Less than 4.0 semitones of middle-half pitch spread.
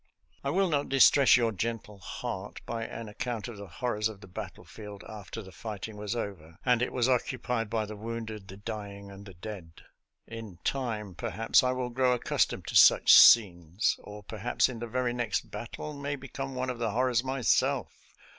Yes: average, 3.4 semitones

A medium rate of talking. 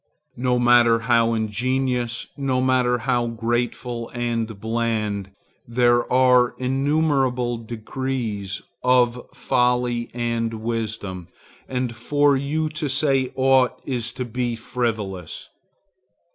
No: slow, 105 wpm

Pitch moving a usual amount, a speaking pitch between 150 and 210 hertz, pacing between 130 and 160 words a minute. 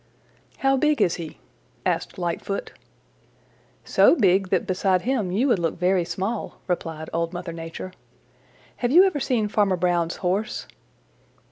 Yes: average, 4.3 semitones; medium, 185 Hz; average, 140 wpm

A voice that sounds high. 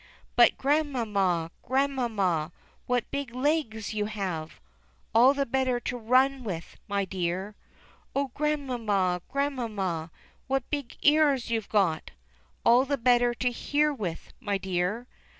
Yes: high, 235 Hz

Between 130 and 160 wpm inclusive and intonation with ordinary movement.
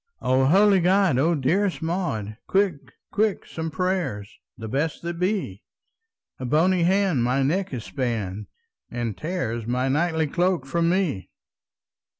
No: average, 140 wpm; wide, 6.6 semitones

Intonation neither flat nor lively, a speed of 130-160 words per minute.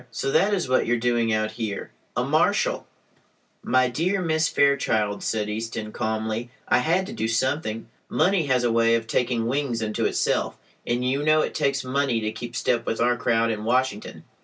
No: average, 3.6 semitones; average, 190 wpm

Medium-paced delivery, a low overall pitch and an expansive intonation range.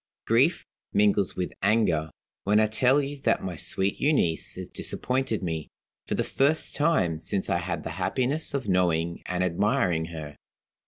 Yes: average, 160 wpm; very low, 95 Hz; wide, 7.0 semitones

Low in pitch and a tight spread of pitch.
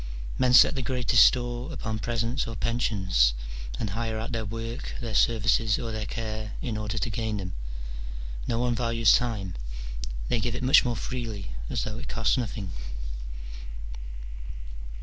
Yes: low, 115 Hz; narrow, 2.1 semitones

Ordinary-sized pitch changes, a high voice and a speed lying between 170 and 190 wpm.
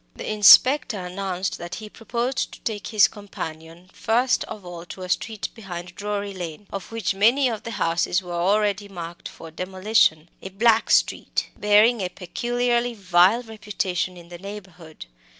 No: average, 3.8 semitones; high, 200 Hz; average, 160 wpm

